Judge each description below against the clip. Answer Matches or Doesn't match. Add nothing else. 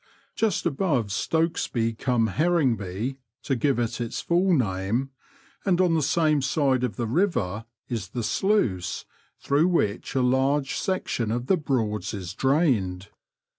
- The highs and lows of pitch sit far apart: Matches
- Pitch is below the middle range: Matches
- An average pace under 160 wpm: Matches